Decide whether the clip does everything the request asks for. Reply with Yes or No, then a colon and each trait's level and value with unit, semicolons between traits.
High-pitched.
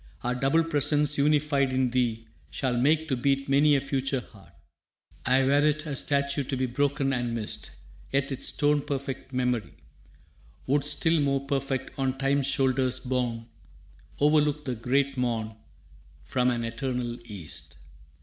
No: low, 135 Hz